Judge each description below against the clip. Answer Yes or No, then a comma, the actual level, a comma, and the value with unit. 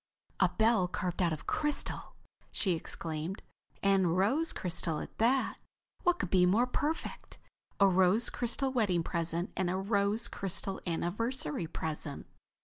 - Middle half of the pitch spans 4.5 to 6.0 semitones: Yes, average, 4.8 semitones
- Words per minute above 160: No, average, 140 wpm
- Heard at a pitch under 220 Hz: Yes, high, 190 Hz